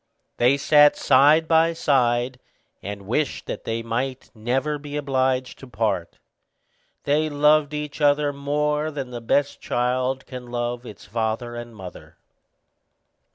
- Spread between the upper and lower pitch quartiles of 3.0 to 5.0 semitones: Yes, average, 3.5 semitones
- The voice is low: Yes, low, 130 Hz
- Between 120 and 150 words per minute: Yes, average, 140 wpm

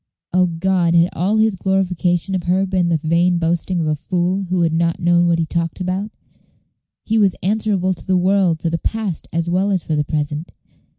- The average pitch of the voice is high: No, medium, 175 Hz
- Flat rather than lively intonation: Yes, narrow, 2.2 semitones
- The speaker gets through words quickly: Yes, fast, 210 wpm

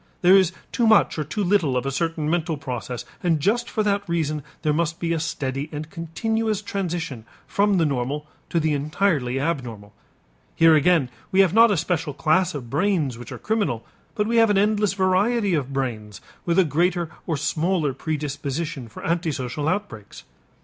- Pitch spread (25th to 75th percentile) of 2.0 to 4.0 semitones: No, average, 5.2 semitones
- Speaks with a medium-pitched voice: Yes, medium, 165 Hz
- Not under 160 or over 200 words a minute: Yes, average, 180 wpm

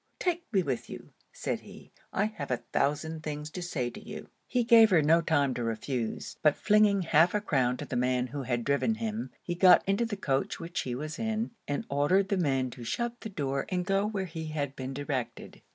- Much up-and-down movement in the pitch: Yes, wide, 6.7 semitones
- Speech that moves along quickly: Yes, fast, 220 wpm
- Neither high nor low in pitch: Yes, medium, 160 Hz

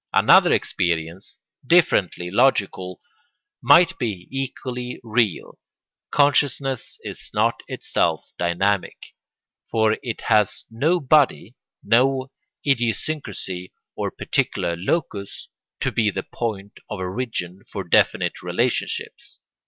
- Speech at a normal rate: No, slow, 100 wpm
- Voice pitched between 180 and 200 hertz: No, low, 110 Hz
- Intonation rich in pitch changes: Yes, wide, 6.0 semitones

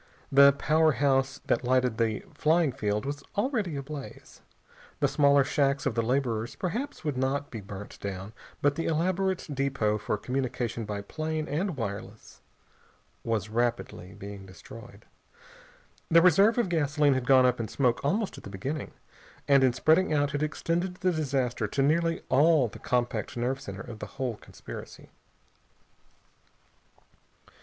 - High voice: No, low, 135 Hz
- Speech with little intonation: No, average, 5.2 semitones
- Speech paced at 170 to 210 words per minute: No, average, 150 wpm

